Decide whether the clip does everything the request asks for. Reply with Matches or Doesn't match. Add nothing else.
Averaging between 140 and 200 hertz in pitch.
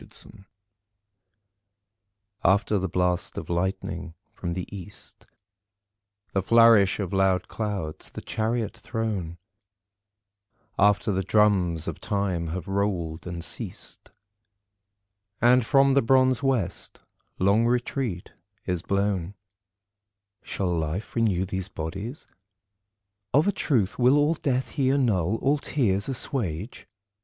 Doesn't match